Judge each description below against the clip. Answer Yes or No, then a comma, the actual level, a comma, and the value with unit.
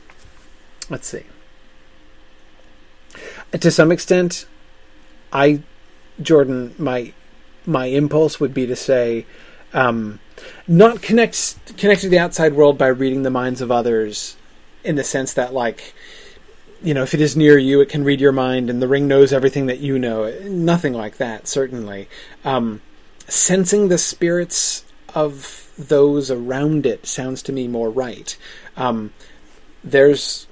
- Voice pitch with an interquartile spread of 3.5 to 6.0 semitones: Yes, average, 5.3 semitones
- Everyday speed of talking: Yes, average, 145 wpm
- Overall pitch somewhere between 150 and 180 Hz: No, low, 135 Hz